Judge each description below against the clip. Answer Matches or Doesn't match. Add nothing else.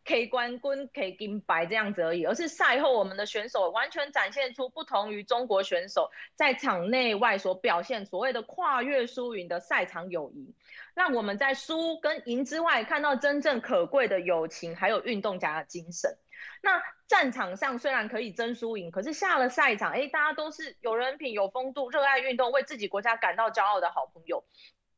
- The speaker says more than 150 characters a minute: Matches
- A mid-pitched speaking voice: Doesn't match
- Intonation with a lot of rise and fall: Matches